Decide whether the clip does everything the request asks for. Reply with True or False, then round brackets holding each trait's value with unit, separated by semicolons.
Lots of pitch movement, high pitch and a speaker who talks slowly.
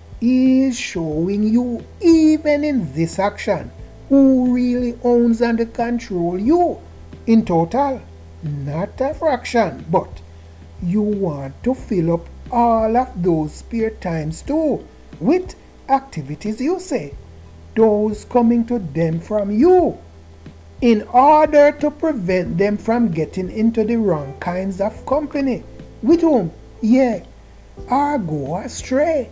True (7.7 semitones; 225 Hz; 120 wpm)